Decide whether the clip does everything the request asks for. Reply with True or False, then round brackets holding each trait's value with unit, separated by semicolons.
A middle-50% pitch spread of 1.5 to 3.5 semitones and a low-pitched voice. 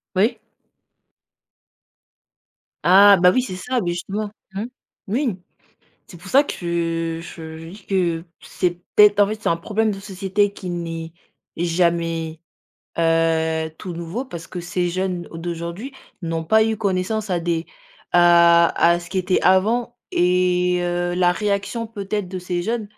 False (3.1 semitones; 180 Hz)